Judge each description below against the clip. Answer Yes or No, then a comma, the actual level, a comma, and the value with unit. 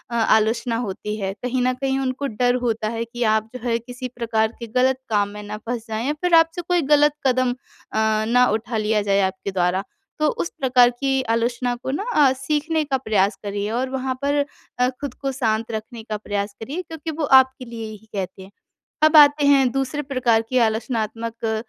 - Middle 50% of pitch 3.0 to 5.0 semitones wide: Yes, average, 3.6 semitones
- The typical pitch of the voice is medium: No, high, 240 Hz